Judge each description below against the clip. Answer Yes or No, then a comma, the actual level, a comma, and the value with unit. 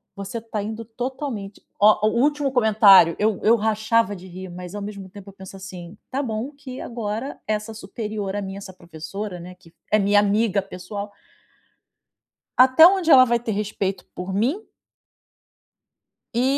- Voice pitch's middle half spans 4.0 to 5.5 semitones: No, average, 3.1 semitones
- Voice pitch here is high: Yes, high, 210 Hz